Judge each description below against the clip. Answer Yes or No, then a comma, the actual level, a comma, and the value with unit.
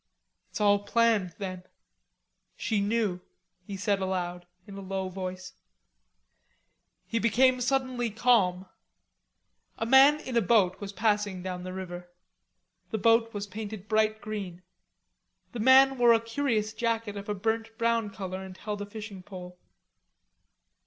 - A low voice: No, high, 210 Hz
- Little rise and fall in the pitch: No, average, 3.4 semitones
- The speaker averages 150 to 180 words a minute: No, average, 140 wpm